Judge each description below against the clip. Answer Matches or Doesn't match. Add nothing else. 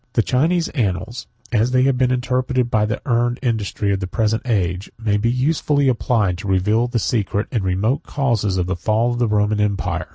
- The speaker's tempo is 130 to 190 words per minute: Doesn't match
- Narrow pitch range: Doesn't match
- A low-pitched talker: Matches